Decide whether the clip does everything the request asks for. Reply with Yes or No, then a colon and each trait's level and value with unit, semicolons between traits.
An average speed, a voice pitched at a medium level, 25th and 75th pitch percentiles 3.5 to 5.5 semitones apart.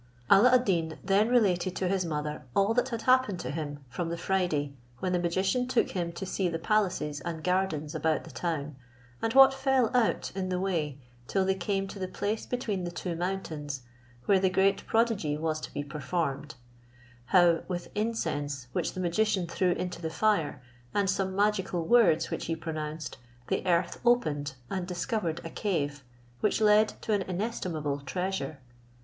Yes: average, 180 wpm; medium, 180 Hz; average, 4.3 semitones